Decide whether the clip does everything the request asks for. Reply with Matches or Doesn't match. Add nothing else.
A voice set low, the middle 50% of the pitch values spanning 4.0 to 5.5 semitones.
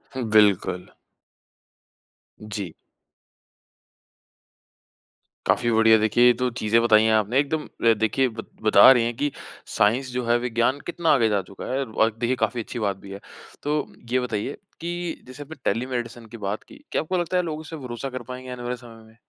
Doesn't match